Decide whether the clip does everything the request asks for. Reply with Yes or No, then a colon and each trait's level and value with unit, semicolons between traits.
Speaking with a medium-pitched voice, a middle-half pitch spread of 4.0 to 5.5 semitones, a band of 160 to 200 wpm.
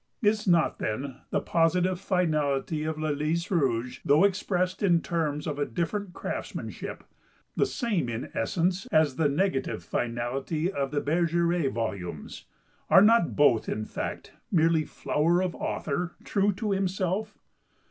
No: medium, 165 Hz; average, 4.5 semitones; average, 140 wpm